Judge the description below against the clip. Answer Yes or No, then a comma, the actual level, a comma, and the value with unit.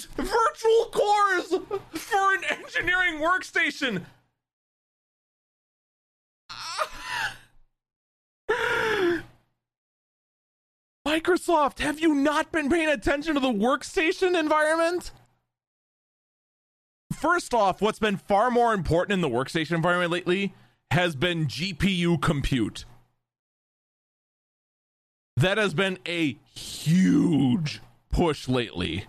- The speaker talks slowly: Yes, slow, 85 wpm